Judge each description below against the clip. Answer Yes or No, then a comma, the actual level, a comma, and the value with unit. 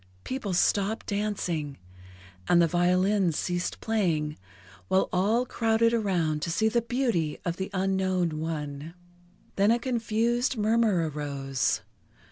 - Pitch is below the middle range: No, high, 190 Hz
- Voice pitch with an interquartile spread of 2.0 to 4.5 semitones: No, average, 5.2 semitones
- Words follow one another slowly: Yes, slow, 120 wpm